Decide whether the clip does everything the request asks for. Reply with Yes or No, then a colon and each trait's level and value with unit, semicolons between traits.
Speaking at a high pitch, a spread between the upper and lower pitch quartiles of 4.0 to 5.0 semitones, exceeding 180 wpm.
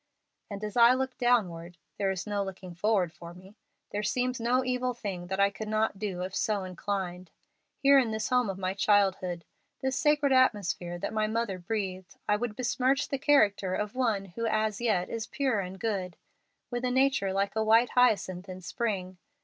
Yes: high, 210 Hz; average, 4.4 semitones; average, 190 wpm